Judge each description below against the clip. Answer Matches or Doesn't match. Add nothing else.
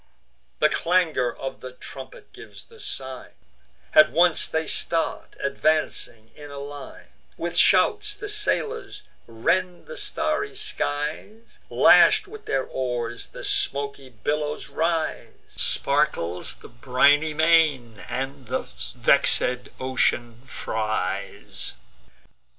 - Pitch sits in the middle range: Matches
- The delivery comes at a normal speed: Doesn't match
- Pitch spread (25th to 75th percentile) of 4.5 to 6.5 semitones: Matches